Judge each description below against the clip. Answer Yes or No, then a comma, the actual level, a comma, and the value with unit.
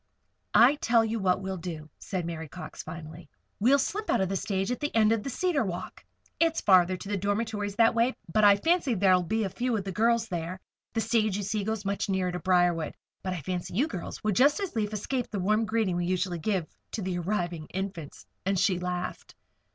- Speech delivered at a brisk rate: Yes, fast, 220 wpm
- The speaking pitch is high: Yes, high, 200 Hz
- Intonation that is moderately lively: Yes, average, 3.9 semitones